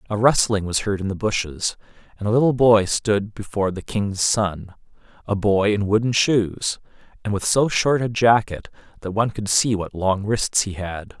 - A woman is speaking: No, male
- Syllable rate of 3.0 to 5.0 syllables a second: Yes, 4.7 syllables/s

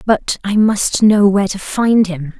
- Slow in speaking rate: No, average, 200 wpm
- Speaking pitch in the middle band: No, high, 200 Hz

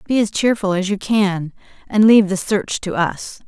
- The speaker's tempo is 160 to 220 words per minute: Yes, fast, 205 wpm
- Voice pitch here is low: No, high, 200 Hz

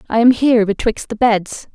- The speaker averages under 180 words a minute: No, fast, 205 wpm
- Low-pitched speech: No, high, 225 Hz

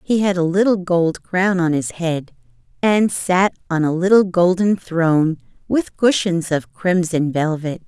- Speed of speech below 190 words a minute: Yes, average, 160 wpm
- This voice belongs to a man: No, female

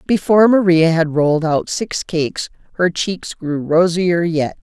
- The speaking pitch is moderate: Yes, medium, 170 Hz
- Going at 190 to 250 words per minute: No, average, 155 wpm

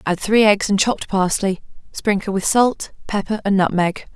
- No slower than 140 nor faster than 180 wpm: Yes, average, 175 wpm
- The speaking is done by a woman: Yes, female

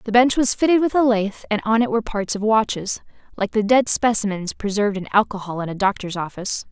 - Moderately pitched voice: No, high, 215 Hz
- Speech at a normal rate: No, fast, 225 wpm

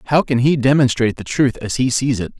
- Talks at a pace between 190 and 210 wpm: No, fast, 250 wpm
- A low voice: Yes, low, 130 Hz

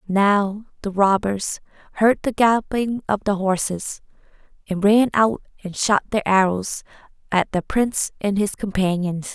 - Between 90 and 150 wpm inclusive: Yes, average, 140 wpm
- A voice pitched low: No, high, 200 Hz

